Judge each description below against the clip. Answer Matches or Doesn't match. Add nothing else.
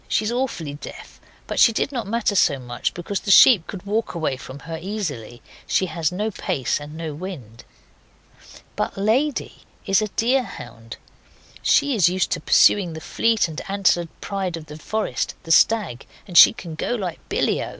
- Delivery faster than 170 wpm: Matches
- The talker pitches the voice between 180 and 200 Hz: Matches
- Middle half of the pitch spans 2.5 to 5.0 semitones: Doesn't match